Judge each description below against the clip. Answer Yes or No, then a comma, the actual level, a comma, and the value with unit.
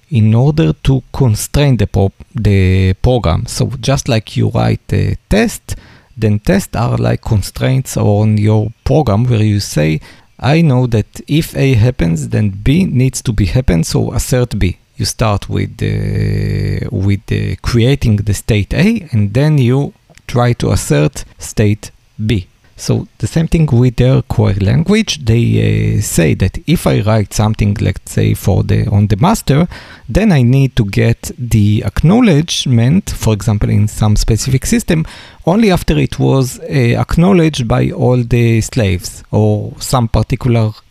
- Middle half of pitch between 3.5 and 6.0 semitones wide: Yes, average, 4.2 semitones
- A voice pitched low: Yes, low, 115 Hz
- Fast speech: No, average, 160 wpm